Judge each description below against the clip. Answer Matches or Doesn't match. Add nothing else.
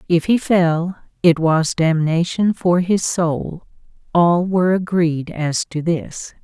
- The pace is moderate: Doesn't match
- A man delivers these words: Doesn't match